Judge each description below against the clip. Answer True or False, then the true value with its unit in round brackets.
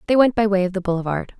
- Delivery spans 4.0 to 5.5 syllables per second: False (7.4 syllables/s)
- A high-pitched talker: True (200 Hz)